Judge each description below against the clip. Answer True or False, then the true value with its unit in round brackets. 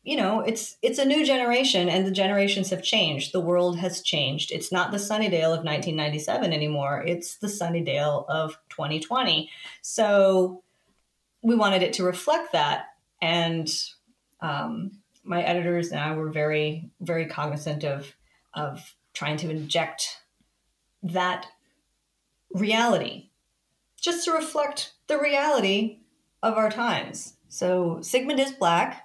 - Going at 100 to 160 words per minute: True (140 wpm)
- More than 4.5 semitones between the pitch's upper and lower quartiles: True (5.6 semitones)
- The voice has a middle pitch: True (180 Hz)